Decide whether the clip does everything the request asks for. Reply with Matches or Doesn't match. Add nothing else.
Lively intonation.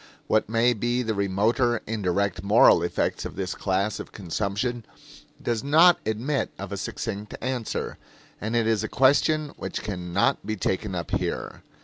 Doesn't match